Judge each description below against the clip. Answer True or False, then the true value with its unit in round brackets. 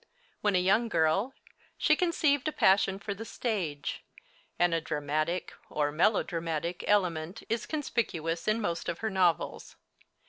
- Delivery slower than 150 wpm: True (140 wpm)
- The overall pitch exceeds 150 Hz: True (185 Hz)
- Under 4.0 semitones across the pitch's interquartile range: False (5.2 semitones)